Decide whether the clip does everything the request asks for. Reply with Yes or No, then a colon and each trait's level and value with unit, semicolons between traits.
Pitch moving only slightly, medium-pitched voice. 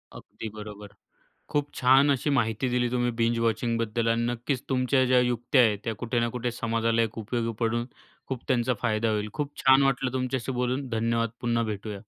No: narrow, 2.0 semitones; low, 120 Hz